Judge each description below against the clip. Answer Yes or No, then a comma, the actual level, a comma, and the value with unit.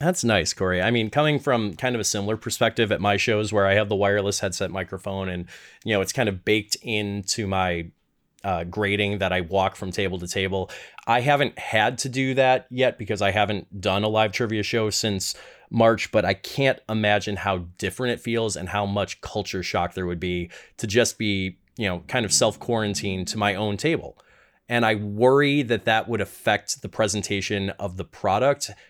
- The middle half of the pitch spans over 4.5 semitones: No, average, 3.0 semitones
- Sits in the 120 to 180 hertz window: No, low, 105 Hz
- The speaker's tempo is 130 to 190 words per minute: No, fast, 205 wpm